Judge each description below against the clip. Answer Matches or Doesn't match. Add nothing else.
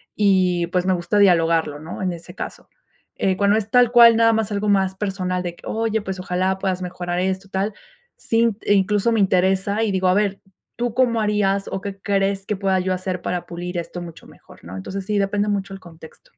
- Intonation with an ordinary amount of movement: Doesn't match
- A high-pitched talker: Matches